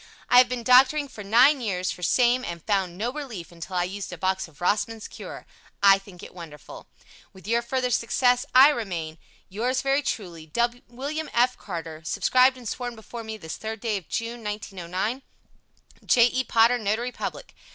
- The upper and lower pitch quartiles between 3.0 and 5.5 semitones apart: Yes, average, 5.1 semitones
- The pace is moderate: Yes, average, 180 wpm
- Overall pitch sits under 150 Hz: No, high, 225 Hz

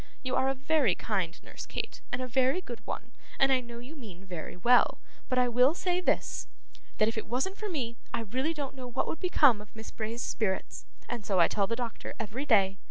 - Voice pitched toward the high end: Yes, high, 245 Hz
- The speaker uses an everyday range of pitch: Yes, average, 3.8 semitones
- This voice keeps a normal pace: No, fast, 230 wpm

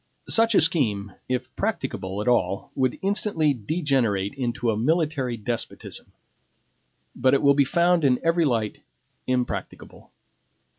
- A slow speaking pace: Yes, slow, 130 wpm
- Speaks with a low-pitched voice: Yes, low, 130 Hz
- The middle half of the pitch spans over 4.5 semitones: Yes, wide, 5.5 semitones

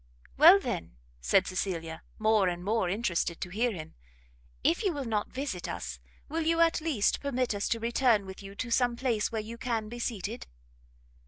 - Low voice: No, high, 220 Hz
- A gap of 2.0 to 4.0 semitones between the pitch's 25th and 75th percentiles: No, average, 4.9 semitones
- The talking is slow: No, average, 185 wpm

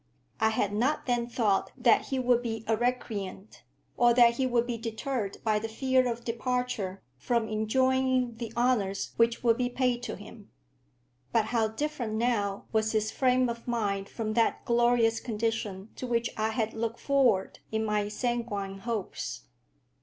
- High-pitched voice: Yes, high, 230 Hz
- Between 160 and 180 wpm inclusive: Yes, average, 165 wpm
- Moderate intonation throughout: No, narrow, 2.2 semitones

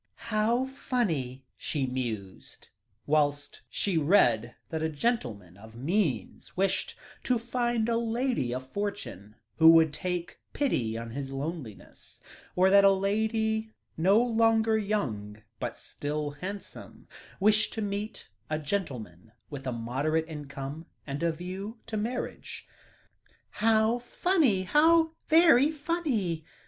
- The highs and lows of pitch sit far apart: Yes, wide, 8.5 semitones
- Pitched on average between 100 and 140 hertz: No, medium, 185 Hz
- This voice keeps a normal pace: No, slow, 125 wpm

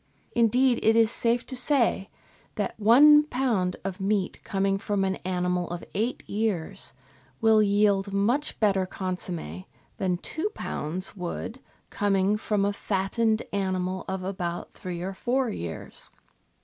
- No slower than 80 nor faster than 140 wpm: Yes, slow, 135 wpm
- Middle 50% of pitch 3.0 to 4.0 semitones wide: Yes, average, 3.3 semitones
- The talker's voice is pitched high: Yes, high, 200 Hz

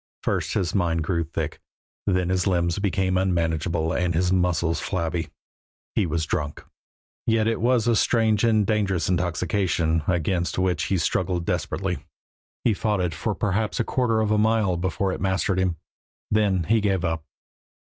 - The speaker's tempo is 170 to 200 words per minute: No, average, 160 wpm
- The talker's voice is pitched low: Yes, very low, 95 Hz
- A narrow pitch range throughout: No, average, 3.6 semitones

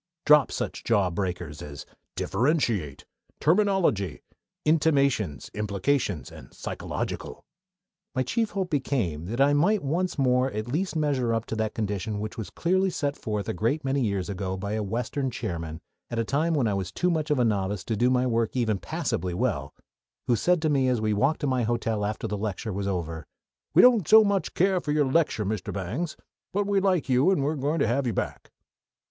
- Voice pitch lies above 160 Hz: No, low, 125 Hz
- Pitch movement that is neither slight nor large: No, wide, 6.6 semitones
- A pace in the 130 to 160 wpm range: No, average, 195 wpm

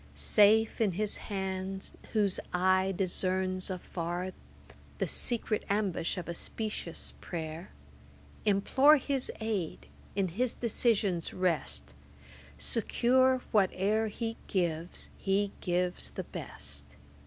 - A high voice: Yes, high, 195 Hz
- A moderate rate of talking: No, slow, 105 wpm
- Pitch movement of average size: Yes, average, 3.4 semitones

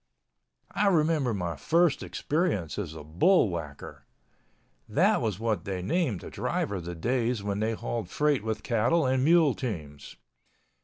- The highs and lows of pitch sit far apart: Yes, wide, 8.7 semitones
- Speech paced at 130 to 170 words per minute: Yes, average, 140 wpm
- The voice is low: Yes, low, 110 Hz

